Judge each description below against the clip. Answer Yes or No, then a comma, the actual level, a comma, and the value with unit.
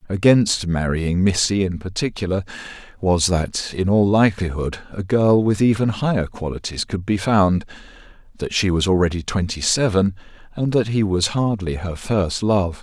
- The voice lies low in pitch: Yes, very low, 95 Hz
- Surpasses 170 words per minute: No, average, 155 wpm